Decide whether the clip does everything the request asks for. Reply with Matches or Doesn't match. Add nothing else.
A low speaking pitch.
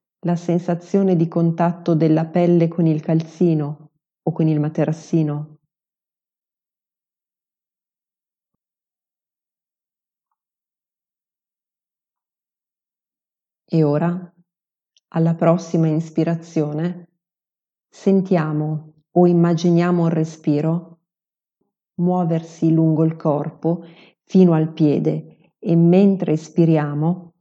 Doesn't match